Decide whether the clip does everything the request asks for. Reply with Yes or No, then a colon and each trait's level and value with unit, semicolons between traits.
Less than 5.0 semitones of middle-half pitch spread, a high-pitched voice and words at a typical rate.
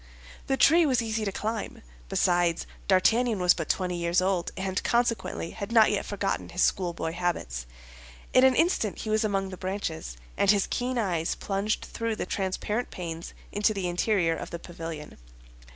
Yes: average, 3.9 semitones; high, 195 Hz; average, 170 wpm